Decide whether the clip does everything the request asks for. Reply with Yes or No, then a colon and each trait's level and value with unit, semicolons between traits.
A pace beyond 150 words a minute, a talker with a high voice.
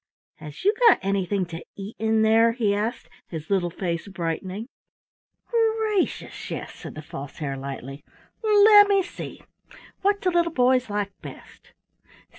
No: average, 140 wpm; high, 210 Hz